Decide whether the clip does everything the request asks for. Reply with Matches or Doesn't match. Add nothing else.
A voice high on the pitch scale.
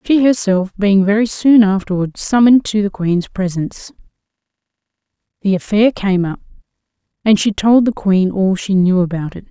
Matches